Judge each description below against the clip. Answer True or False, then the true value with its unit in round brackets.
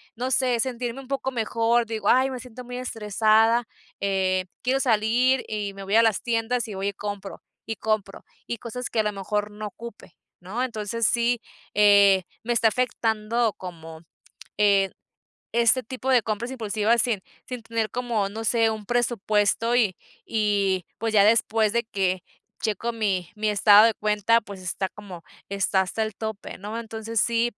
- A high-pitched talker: True (220 Hz)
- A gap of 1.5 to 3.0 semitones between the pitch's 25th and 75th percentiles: True (2.6 semitones)